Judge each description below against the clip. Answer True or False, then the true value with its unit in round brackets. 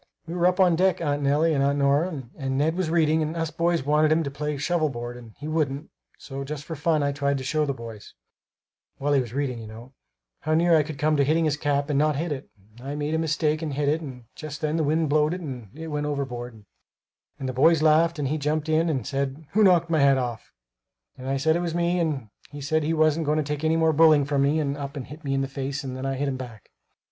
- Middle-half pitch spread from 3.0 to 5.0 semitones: False (2.6 semitones)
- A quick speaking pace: True (270 wpm)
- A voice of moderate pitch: True (150 Hz)